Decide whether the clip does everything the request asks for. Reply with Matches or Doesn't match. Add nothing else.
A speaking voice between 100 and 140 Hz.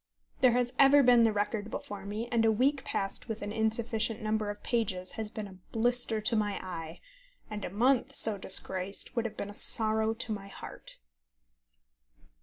Doesn't match